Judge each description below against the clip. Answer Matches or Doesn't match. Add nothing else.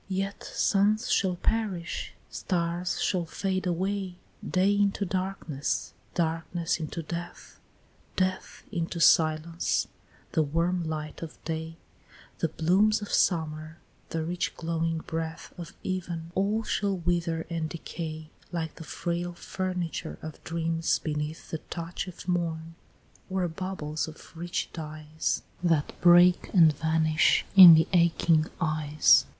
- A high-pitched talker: Doesn't match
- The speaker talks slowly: Matches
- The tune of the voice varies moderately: Doesn't match